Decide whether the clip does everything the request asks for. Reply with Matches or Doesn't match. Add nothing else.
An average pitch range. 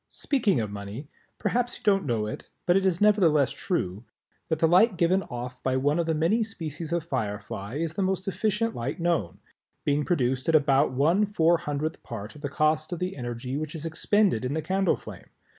Doesn't match